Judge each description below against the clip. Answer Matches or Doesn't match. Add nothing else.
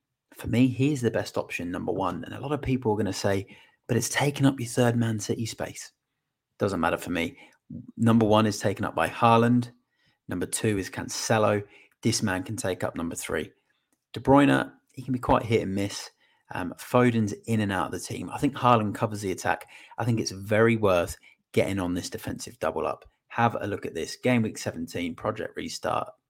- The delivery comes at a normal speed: Doesn't match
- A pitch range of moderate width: Matches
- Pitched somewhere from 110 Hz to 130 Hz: Matches